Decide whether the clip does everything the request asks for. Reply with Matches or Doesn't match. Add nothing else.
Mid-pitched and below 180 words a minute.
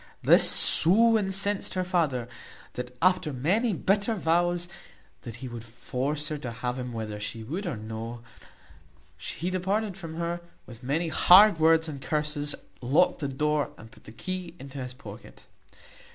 Matches